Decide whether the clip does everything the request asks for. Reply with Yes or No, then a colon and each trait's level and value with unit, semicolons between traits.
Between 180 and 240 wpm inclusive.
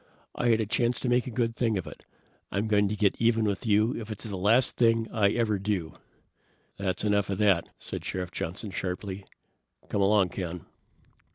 Yes: average, 195 wpm